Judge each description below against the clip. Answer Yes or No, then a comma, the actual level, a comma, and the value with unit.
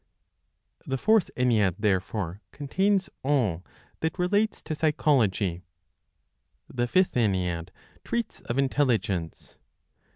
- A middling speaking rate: No, slow, 95 wpm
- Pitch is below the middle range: Yes, low, 125 Hz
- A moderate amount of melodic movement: No, wide, 8.9 semitones